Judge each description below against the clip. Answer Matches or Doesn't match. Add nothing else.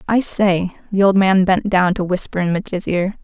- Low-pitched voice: Doesn't match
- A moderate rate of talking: Doesn't match